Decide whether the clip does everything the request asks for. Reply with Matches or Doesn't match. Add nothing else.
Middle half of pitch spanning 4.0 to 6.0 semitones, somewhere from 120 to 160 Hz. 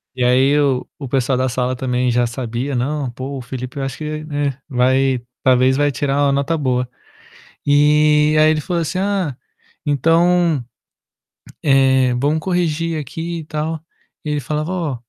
Doesn't match